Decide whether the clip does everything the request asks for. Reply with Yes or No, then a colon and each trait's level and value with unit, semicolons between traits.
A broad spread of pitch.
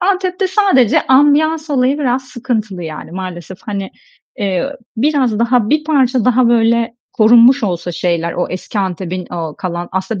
Yes: wide, 6.6 semitones